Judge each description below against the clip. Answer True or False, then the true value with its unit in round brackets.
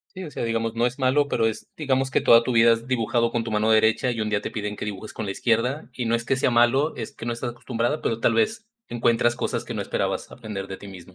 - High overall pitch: False (115 Hz)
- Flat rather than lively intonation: True (2.3 semitones)